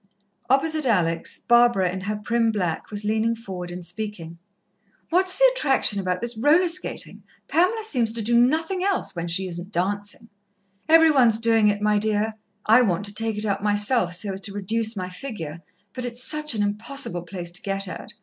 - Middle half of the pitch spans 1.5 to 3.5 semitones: No, average, 4.3 semitones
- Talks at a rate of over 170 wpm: Yes, average, 190 wpm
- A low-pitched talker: No, high, 215 Hz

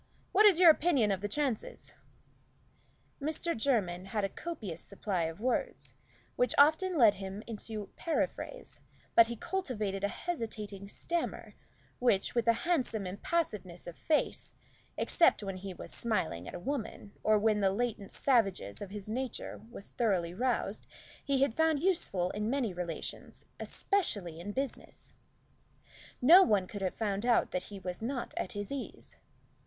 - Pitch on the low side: No, high, 215 Hz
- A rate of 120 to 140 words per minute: No, average, 155 wpm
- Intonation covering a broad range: Yes, wide, 6.0 semitones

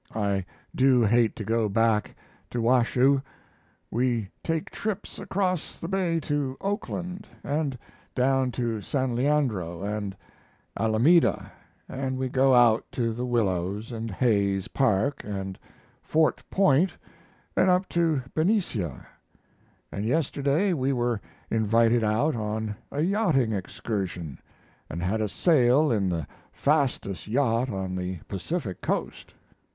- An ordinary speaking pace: No, slow, 125 wpm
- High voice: No, low, 120 Hz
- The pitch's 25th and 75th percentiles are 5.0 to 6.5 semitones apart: Yes, wide, 5.5 semitones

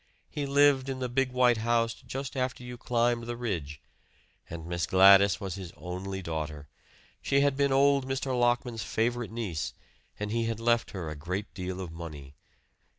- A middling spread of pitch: No, wide, 5.7 semitones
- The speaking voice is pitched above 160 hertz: No, low, 115 Hz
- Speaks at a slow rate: No, average, 175 wpm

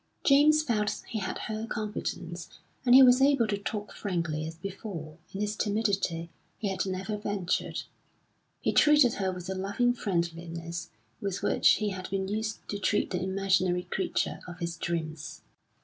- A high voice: Yes, high, 195 Hz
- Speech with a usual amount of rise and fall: Yes, average, 3.6 semitones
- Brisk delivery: No, average, 165 wpm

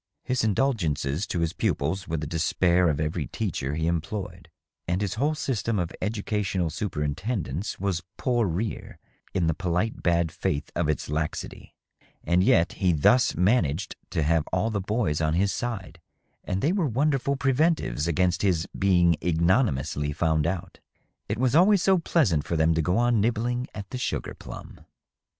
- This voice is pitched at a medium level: No, very low, 90 Hz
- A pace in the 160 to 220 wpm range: Yes, average, 165 wpm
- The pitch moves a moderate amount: No, wide, 5.7 semitones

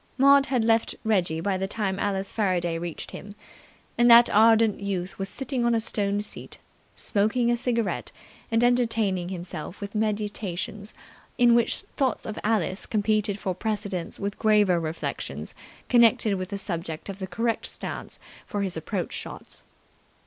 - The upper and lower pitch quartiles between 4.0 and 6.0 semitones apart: No, average, 3.3 semitones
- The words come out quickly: No, average, 155 wpm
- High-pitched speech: Yes, high, 205 Hz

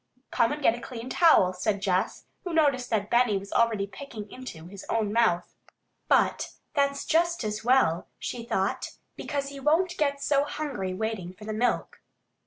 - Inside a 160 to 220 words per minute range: Yes, average, 175 wpm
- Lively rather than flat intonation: Yes, wide, 5.7 semitones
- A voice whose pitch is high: Yes, high, 235 Hz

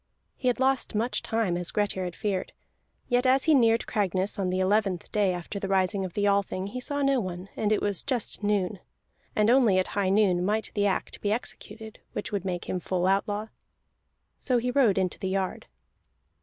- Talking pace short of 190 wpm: No, average, 200 wpm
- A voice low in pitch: No, high, 205 Hz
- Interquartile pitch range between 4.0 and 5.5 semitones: No, average, 3.3 semitones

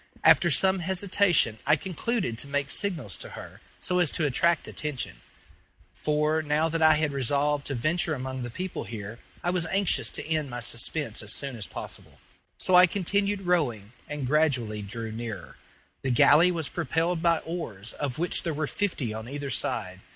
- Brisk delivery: No, average, 180 wpm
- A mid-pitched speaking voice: Yes, medium, 150 Hz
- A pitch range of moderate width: No, wide, 6.0 semitones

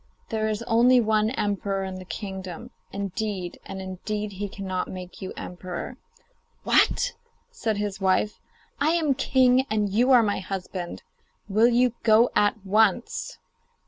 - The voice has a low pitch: No, high, 210 Hz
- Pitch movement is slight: No, average, 3.6 semitones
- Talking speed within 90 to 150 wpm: Yes, average, 145 wpm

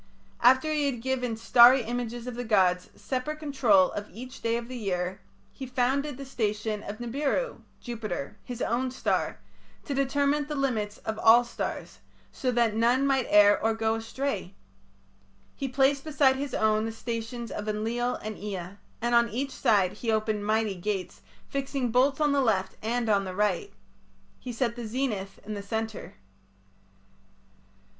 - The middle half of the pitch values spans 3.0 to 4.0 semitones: Yes, average, 3.6 semitones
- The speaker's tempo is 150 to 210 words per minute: Yes, average, 165 wpm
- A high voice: Yes, high, 235 Hz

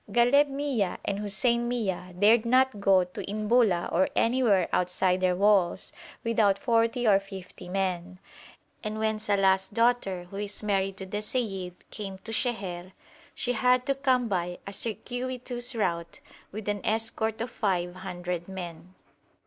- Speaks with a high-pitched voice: Yes, high, 205 Hz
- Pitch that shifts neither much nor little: Yes, average, 4.0 semitones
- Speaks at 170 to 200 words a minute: No, average, 150 wpm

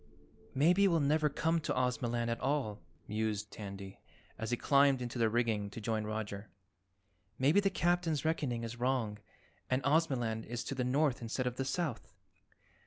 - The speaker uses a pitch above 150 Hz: No, low, 125 Hz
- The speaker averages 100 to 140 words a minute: No, average, 165 wpm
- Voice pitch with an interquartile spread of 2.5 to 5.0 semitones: Yes, average, 4.7 semitones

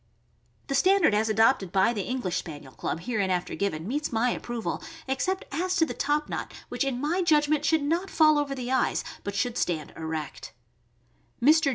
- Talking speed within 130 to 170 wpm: No, average, 180 wpm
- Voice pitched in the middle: No, very high, 255 Hz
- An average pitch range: No, wide, 7.2 semitones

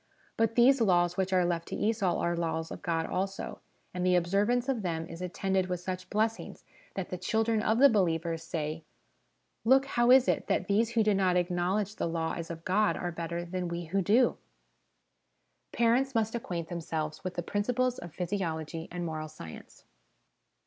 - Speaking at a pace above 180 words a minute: Yes, average, 190 wpm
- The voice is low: No, medium, 185 Hz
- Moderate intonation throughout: Yes, average, 4.4 semitones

